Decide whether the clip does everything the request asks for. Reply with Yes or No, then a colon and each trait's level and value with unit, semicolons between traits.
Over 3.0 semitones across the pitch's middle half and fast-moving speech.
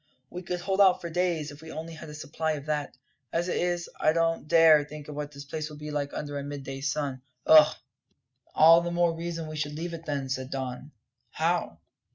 No: narrow, 2.5 semitones; fast, 215 wpm